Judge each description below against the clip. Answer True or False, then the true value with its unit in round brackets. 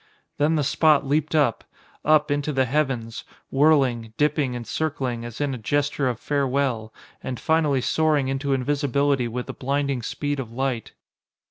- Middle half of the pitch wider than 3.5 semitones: False (2.8 semitones)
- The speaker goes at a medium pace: True (155 wpm)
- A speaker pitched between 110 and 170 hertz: True (140 Hz)